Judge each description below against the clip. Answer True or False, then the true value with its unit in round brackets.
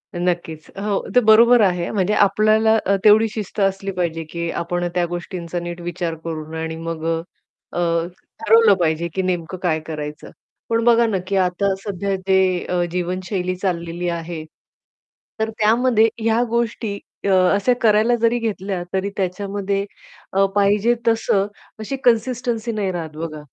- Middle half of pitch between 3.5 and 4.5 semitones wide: True (3.9 semitones)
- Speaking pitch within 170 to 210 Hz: True (190 Hz)